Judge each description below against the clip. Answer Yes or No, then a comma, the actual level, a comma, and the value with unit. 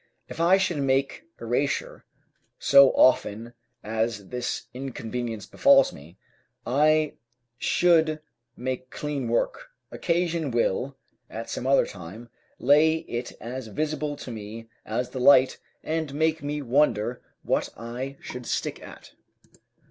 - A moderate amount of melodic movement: Yes, average, 4.7 semitones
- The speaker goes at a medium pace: No, slow, 125 wpm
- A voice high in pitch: No, low, 130 Hz